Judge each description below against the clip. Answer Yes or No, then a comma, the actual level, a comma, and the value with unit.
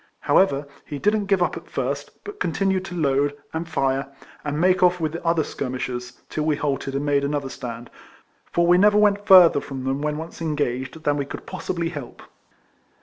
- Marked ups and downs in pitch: No, average, 4.4 semitones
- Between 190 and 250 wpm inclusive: Yes, average, 195 wpm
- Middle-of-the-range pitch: Yes, medium, 150 Hz